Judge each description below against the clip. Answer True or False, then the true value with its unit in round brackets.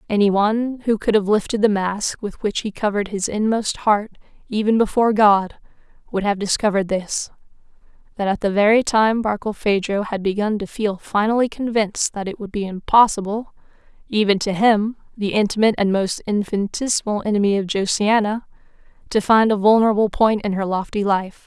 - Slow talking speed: False (160 wpm)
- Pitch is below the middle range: False (210 Hz)